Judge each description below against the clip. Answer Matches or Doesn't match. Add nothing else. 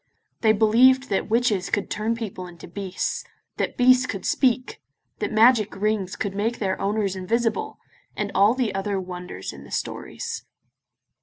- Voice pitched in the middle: Doesn't match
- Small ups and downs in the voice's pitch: Doesn't match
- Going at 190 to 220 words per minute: Doesn't match